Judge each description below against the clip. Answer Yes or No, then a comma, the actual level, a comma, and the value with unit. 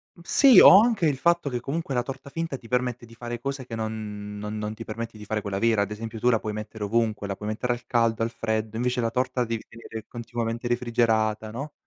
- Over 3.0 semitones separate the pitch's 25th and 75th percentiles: No, narrow, 2.4 semitones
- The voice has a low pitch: Yes, low, 115 Hz